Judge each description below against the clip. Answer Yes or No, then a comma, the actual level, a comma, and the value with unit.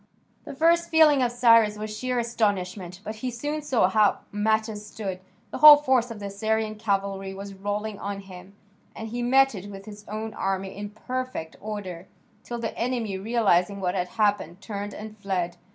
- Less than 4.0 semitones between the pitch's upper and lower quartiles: Yes, average, 3.2 semitones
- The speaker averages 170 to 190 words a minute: Yes, average, 180 wpm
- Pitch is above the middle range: Yes, high, 210 Hz